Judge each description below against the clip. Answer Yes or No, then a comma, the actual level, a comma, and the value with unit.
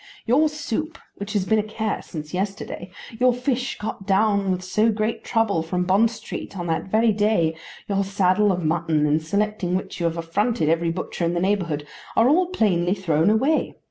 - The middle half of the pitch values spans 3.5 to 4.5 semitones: Yes, average, 4.2 semitones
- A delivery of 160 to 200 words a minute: Yes, average, 190 wpm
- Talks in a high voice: Yes, high, 200 Hz